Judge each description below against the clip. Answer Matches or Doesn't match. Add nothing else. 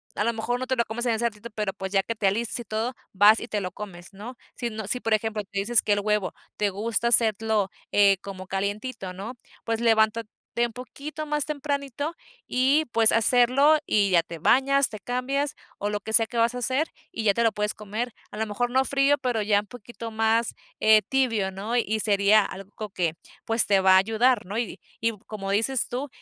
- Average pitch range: Matches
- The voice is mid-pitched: Doesn't match